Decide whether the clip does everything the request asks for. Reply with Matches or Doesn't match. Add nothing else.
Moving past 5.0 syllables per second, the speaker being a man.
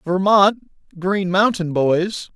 Doesn't match